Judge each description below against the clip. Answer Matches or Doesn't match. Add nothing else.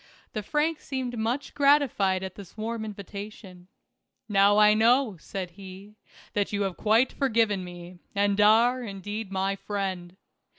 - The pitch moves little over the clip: Doesn't match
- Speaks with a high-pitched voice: Matches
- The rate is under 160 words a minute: Matches